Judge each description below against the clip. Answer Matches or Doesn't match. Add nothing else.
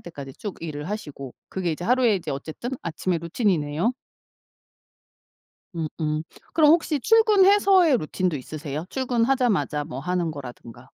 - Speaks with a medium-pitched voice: Matches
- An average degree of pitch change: Doesn't match